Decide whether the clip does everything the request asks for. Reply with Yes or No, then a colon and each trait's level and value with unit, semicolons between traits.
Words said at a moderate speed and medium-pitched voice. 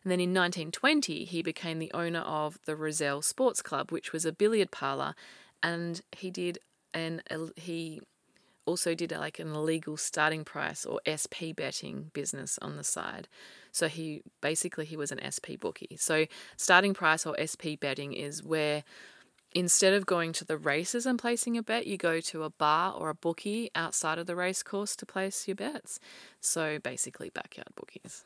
Yes: average, 180 wpm; medium, 165 Hz